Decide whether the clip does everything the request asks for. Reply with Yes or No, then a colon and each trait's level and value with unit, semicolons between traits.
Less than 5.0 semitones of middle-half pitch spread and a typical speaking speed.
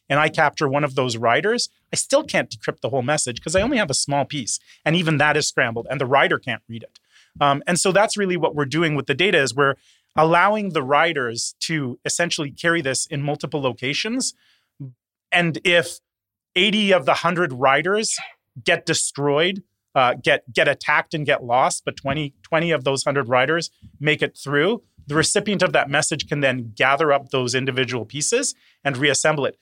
Yes: average, 4.2 semitones; average, 195 wpm